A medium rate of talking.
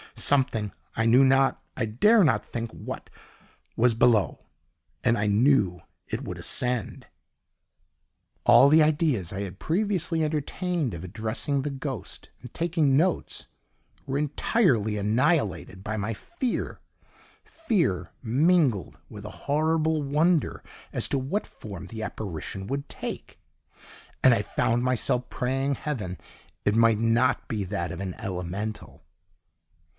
No: slow, 130 wpm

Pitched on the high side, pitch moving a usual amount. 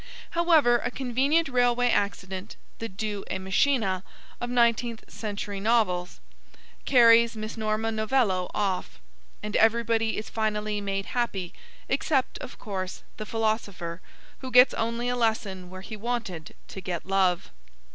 Yes: high, 220 Hz; average, 3.6 semitones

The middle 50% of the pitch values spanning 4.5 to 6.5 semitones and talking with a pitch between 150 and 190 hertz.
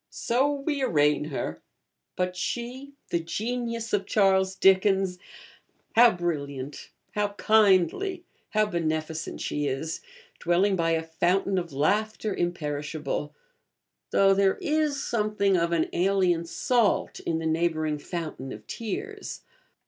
Yes: average, 4.9 semitones; medium, 185 Hz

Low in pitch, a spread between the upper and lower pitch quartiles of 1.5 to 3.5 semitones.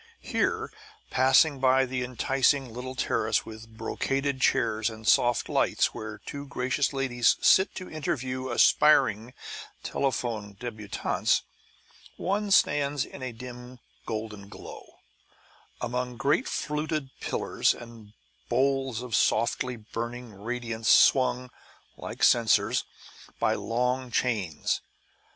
Yes: low, 125 Hz; average, 2.9 semitones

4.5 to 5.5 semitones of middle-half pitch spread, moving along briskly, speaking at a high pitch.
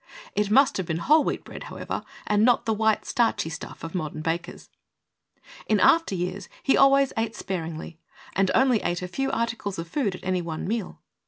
No: average, 5.1 semitones; average, 190 wpm; high, 200 Hz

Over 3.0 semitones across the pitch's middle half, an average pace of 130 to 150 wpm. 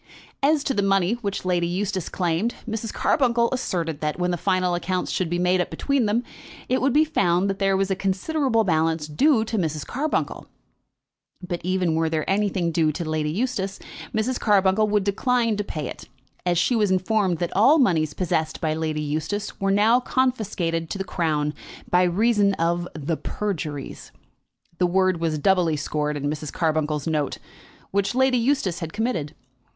No: average, 4.9 semitones; average, 175 wpm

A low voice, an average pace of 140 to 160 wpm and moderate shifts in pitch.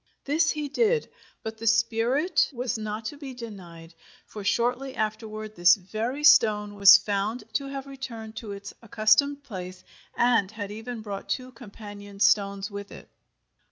No: high, 220 Hz; average, 155 wpm; average, 3.8 semitones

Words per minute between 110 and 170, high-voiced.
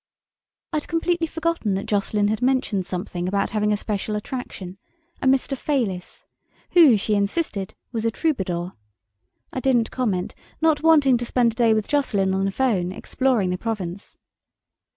Yes: average, 155 wpm; high, 220 Hz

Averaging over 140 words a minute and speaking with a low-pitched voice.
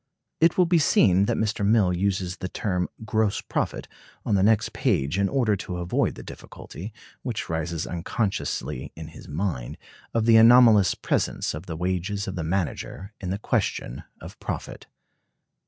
Yes: average, 165 wpm; very low, 95 Hz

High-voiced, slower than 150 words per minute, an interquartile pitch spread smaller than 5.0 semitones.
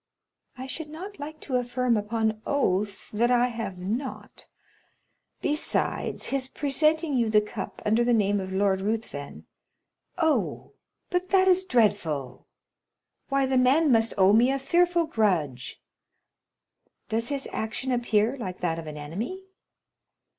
No: high, 235 Hz; average, 140 wpm; wide, 5.6 semitones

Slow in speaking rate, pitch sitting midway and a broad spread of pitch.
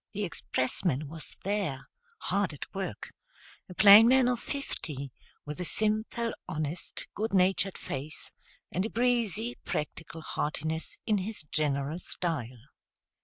Yes: slow, 125 wpm; medium, 180 Hz; wide, 6.0 semitones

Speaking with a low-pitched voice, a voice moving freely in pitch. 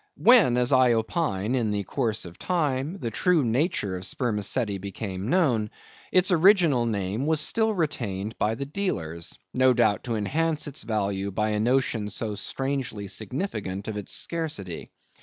Yes: low, 120 Hz; wide, 6.5 semitones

